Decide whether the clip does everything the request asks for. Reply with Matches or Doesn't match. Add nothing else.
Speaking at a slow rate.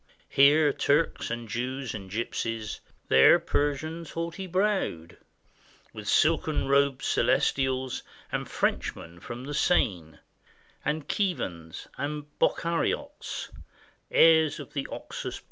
Matches